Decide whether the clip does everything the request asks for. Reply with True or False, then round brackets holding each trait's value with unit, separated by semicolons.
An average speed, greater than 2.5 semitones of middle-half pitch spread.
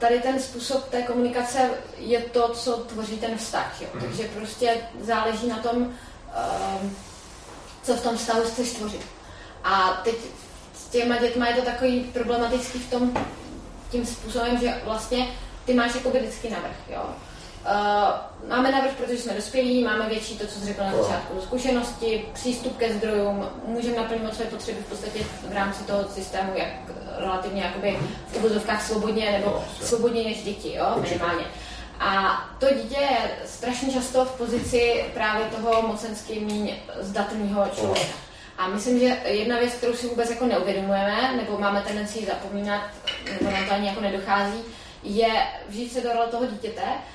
True (160 wpm; 2.9 semitones)